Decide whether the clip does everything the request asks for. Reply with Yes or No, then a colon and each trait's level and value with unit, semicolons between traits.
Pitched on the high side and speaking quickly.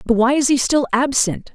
Yes: very high, 260 Hz; fast, 235 wpm